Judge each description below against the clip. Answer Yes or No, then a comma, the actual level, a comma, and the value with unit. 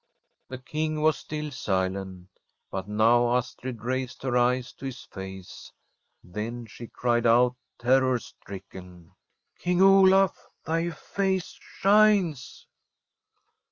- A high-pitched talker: No, low, 125 Hz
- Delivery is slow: Yes, slow, 115 wpm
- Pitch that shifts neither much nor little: No, wide, 6.6 semitones